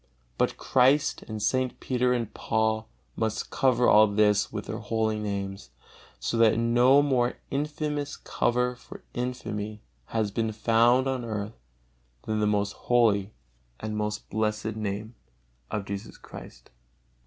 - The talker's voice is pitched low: Yes, low, 110 Hz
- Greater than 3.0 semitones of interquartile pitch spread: No, average, 2.7 semitones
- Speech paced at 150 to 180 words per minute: No, slow, 135 wpm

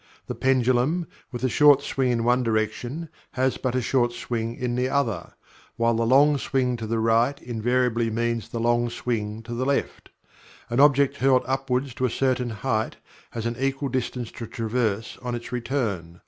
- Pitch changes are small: Yes, narrow, 2.3 semitones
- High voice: No, low, 120 Hz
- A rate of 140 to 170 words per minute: No, average, 180 wpm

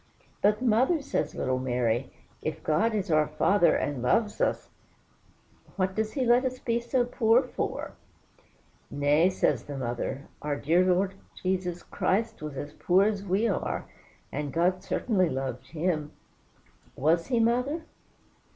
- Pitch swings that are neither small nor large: No, wide, 7.3 semitones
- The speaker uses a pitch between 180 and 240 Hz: Yes, medium, 185 Hz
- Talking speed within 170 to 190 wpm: No, average, 150 wpm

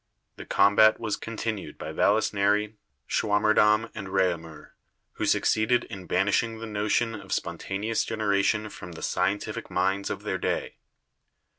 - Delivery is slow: Yes, slow, 130 wpm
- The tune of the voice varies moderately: No, narrow, 2.0 semitones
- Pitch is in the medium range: No, low, 105 Hz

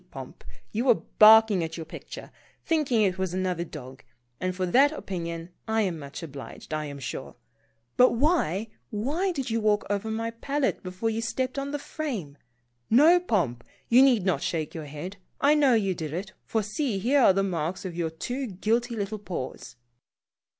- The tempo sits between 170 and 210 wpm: Yes, average, 185 wpm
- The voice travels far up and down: Yes, wide, 6.2 semitones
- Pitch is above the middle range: Yes, high, 205 Hz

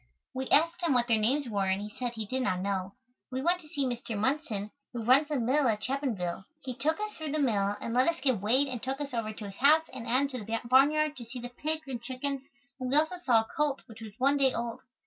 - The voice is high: Yes, very high, 255 Hz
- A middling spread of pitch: Yes, average, 4.2 semitones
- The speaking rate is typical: No, fast, 265 wpm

